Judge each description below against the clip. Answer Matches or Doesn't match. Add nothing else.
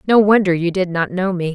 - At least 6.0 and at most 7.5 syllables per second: Doesn't match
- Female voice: Matches